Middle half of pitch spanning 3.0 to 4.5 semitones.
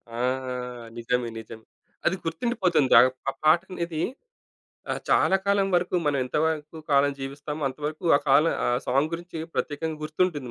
Yes: average, 3.5 semitones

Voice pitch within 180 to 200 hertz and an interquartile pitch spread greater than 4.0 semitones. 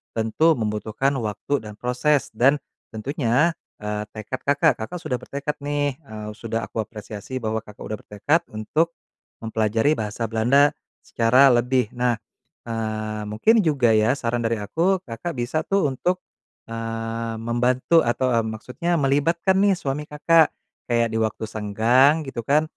No: low, 120 Hz; average, 4.6 semitones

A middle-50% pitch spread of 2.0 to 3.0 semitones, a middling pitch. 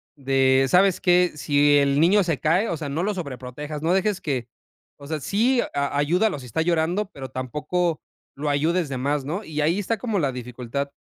No: average, 4.4 semitones; medium, 150 Hz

